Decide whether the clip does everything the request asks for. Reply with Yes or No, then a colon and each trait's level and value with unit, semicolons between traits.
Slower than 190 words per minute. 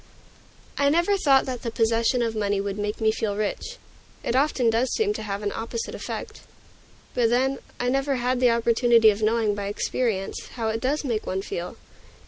No: average, 195 wpm